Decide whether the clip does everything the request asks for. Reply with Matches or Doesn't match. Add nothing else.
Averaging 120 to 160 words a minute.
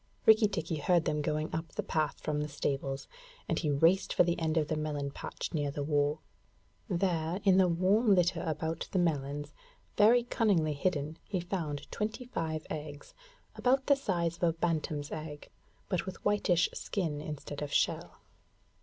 Doesn't match